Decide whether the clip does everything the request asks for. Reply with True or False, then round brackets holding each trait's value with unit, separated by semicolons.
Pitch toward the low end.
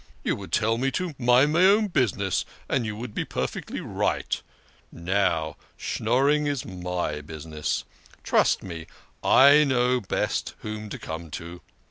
True (110 Hz)